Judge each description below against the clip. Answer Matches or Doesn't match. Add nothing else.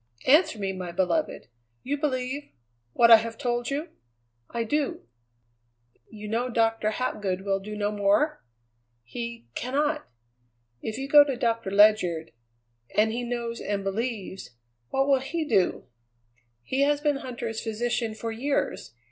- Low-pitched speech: Doesn't match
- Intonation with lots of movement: Doesn't match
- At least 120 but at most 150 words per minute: Matches